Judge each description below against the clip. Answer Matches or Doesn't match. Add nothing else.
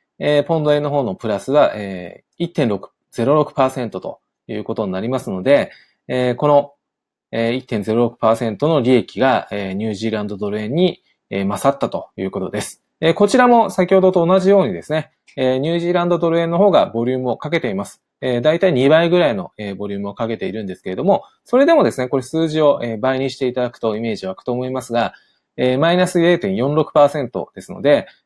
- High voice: Doesn't match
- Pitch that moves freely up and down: Matches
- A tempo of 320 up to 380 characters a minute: Doesn't match